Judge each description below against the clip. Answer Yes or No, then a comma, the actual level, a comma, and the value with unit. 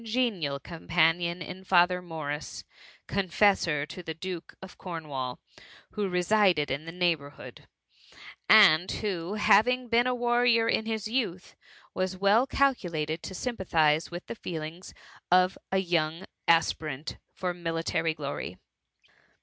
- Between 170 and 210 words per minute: No, slow, 135 wpm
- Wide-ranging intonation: No, average, 4.2 semitones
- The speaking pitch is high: No, medium, 180 Hz